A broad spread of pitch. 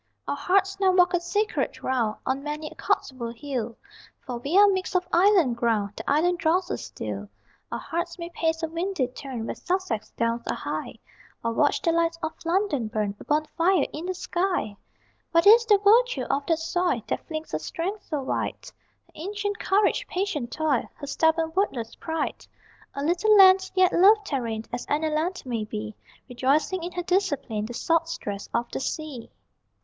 Yes: wide, 6.5 semitones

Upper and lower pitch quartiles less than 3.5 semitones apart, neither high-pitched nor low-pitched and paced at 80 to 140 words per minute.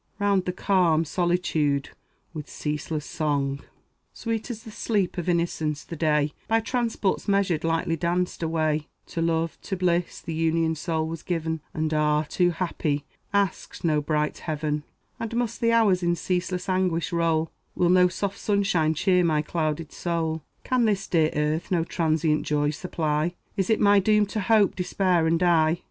No: average, 3.1 semitones; medium, 170 Hz; average, 165 wpm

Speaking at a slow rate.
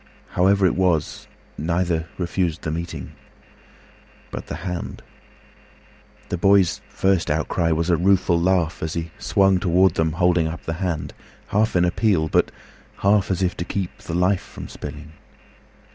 Yes: slow, 130 wpm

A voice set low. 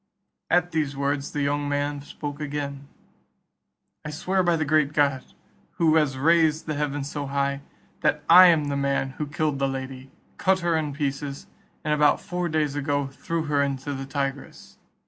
No: medium, 145 Hz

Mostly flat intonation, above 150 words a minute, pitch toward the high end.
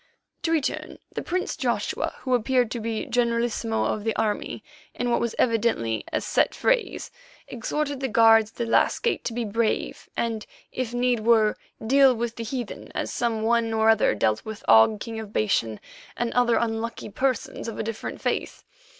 Yes: narrow, 1.8 semitones; average, 180 wpm; high, 230 Hz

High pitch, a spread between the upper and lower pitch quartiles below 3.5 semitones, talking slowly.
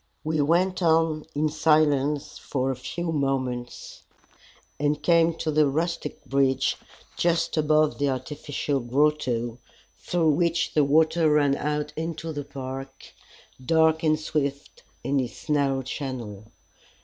No: medium, 150 Hz; average, 2.8 semitones; slow, 125 wpm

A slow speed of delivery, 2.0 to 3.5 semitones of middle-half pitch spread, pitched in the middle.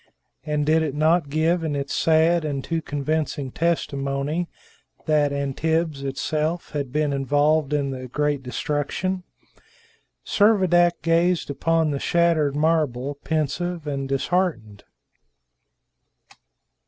Yes: slow, 110 wpm; average, 2.8 semitones; medium, 150 Hz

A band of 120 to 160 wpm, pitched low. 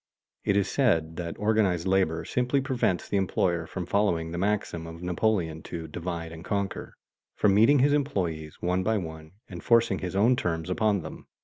No: average, 180 wpm; very low, 90 Hz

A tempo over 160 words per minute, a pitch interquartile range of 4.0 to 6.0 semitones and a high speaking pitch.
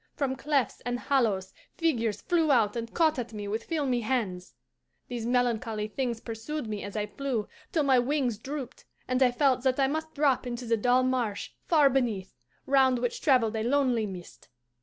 No: average, 180 wpm; average, 3.5 semitones; high, 245 Hz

